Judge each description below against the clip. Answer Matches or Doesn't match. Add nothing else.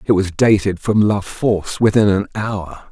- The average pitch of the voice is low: Matches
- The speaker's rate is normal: Matches